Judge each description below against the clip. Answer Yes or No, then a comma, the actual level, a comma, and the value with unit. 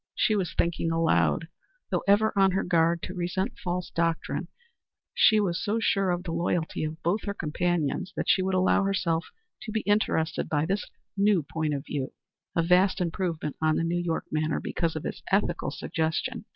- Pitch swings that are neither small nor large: Yes, average, 3.1 semitones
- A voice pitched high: No, medium, 175 Hz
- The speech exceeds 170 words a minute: Yes, average, 185 wpm